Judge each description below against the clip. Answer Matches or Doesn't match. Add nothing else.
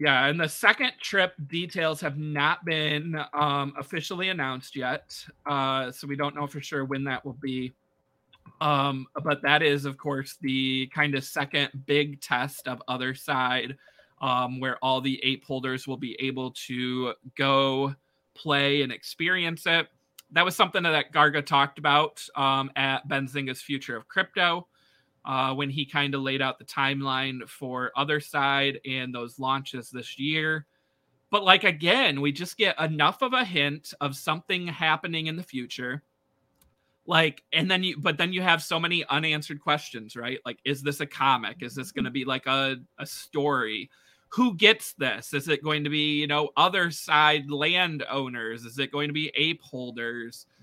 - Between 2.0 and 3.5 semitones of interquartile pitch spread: Matches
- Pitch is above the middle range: Doesn't match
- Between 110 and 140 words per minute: Doesn't match